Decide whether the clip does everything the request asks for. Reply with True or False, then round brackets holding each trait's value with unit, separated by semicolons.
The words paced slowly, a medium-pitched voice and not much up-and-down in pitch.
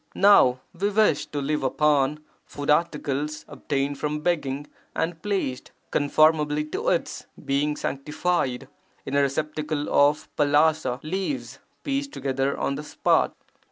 True (125 wpm; 150 Hz; 2.2 semitones)